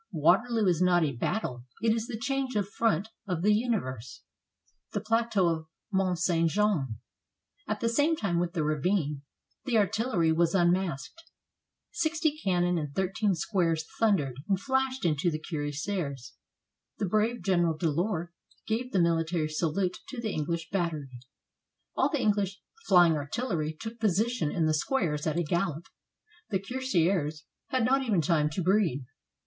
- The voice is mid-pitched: Yes, medium, 180 Hz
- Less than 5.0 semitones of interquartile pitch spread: No, wide, 5.5 semitones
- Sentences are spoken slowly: No, average, 155 wpm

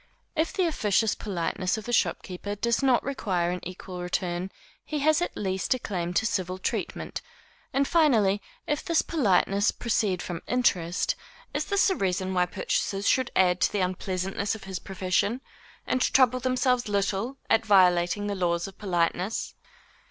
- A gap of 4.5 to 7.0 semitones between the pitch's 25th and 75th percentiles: Yes, average, 5.0 semitones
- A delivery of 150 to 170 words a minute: Yes, average, 160 wpm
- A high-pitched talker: Yes, high, 200 Hz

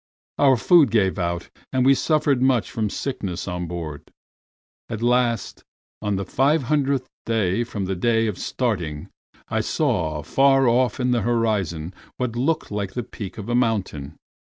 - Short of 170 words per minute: Yes, average, 160 wpm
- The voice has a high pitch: No, low, 115 Hz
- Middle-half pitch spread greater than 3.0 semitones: Yes, average, 5.3 semitones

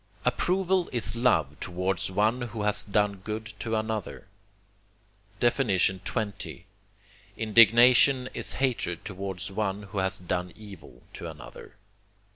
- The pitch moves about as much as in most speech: Yes, average, 3.6 semitones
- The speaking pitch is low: Yes, low, 105 Hz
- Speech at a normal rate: No, slow, 110 wpm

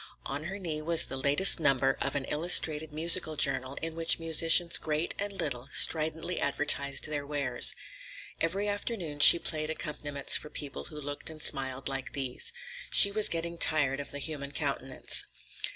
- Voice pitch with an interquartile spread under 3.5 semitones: Yes, average, 2.9 semitones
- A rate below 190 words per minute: Yes, average, 165 wpm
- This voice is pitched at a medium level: Yes, medium, 150 Hz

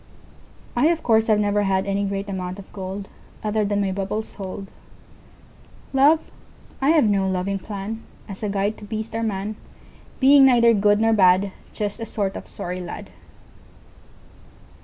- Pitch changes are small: Yes, narrow, 2.2 semitones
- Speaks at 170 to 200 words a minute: No, average, 140 wpm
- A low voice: No, high, 205 Hz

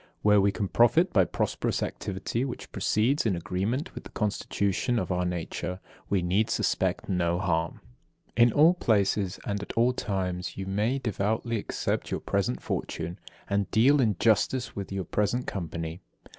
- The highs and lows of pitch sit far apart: No, average, 4.3 semitones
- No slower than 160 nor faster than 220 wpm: Yes, average, 165 wpm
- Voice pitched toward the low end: Yes, low, 100 Hz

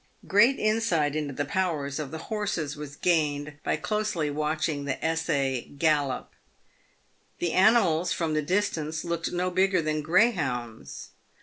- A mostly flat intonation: No, average, 3.9 semitones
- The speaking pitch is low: No, medium, 160 Hz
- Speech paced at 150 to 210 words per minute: No, slow, 135 wpm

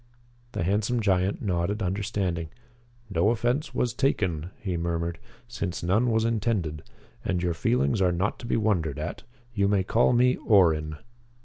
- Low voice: Yes, very low, 95 Hz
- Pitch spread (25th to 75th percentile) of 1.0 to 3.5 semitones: No, average, 4.5 semitones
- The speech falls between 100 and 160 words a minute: Yes, average, 150 wpm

